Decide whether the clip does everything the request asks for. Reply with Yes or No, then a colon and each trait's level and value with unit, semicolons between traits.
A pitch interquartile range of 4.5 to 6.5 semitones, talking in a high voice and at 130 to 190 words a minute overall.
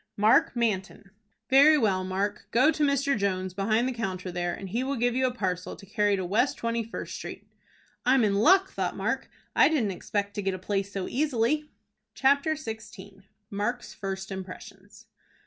Yes: average, 4.8 semitones; high, 210 Hz; average, 180 wpm